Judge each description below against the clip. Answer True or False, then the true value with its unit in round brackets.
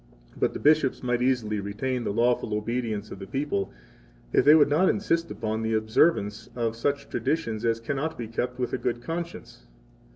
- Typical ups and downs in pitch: True (4.5 semitones)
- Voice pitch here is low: True (120 Hz)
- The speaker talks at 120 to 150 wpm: False (190 wpm)